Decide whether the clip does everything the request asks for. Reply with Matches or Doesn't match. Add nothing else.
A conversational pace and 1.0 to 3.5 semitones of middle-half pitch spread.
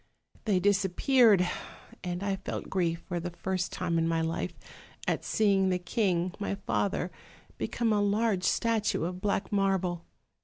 Matches